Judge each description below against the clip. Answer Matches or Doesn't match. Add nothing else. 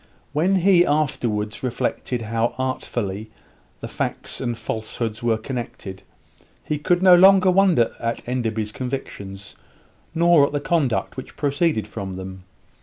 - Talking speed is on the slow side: Matches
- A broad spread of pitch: Matches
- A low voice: Matches